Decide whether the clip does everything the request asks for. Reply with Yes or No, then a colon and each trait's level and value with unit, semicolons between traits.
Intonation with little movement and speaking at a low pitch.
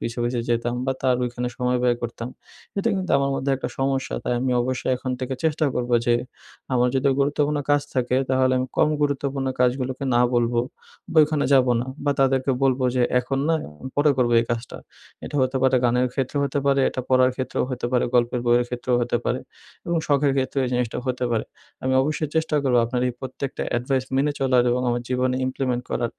Yes: narrow, 1.9 semitones; low, 130 Hz